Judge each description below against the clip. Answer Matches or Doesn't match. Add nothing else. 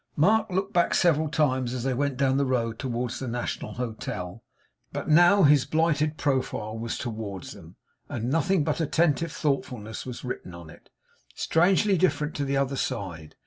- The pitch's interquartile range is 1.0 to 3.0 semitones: Doesn't match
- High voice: Doesn't match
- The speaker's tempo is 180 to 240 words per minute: Doesn't match